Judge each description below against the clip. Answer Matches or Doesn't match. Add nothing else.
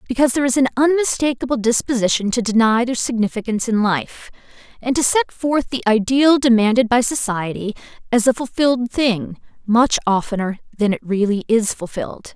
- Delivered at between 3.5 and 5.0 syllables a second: Doesn't match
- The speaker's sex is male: Doesn't match